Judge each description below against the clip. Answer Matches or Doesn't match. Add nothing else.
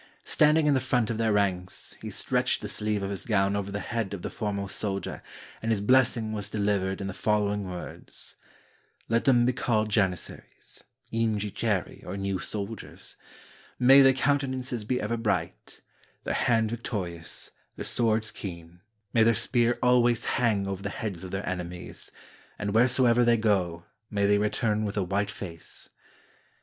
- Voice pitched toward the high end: Doesn't match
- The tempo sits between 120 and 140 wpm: Doesn't match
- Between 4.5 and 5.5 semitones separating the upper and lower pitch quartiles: Doesn't match